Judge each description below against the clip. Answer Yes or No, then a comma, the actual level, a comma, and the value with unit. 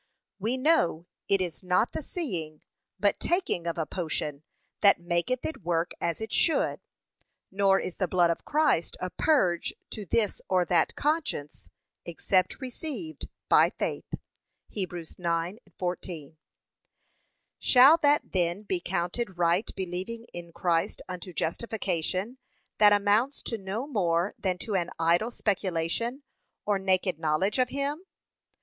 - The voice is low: No, high, 190 Hz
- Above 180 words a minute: No, slow, 135 wpm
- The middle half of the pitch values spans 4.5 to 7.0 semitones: Yes, average, 5.2 semitones